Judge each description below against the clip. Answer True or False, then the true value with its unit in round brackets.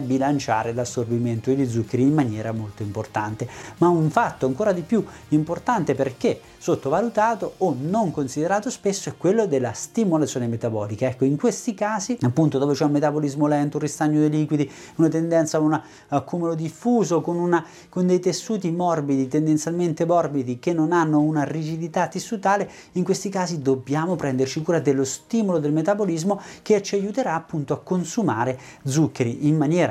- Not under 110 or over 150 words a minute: False (160 wpm)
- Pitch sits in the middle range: True (155 Hz)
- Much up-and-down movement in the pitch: False (4.6 semitones)